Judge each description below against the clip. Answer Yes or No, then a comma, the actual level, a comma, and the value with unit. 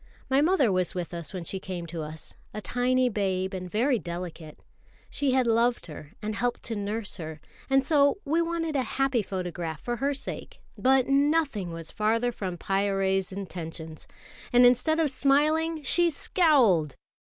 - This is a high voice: Yes, high, 225 Hz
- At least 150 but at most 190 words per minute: Yes, average, 165 wpm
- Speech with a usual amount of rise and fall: No, wide, 7.1 semitones